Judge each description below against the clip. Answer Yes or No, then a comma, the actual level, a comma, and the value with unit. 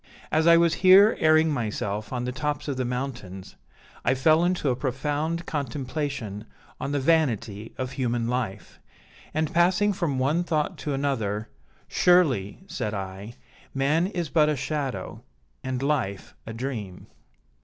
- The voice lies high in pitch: No, low, 135 Hz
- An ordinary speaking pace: Yes, average, 145 wpm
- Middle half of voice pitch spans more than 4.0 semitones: Yes, average, 5.1 semitones